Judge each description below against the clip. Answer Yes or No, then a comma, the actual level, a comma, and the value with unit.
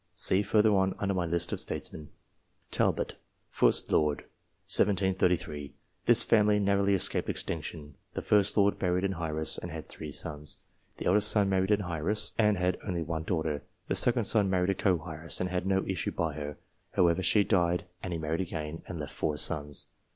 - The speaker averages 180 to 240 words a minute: Yes, average, 190 wpm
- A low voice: Yes, very low, 90 Hz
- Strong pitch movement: No, average, 3.8 semitones